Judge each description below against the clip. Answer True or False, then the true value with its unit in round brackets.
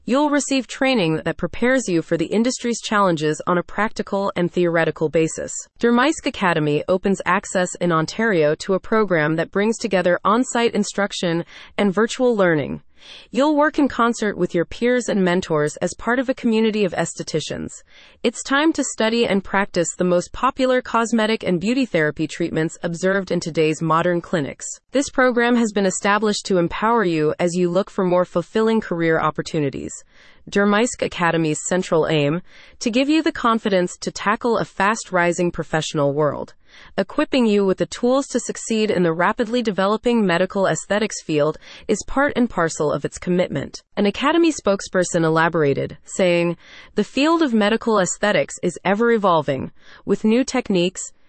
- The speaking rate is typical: True (160 wpm)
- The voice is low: False (195 Hz)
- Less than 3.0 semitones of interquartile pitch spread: False (5.4 semitones)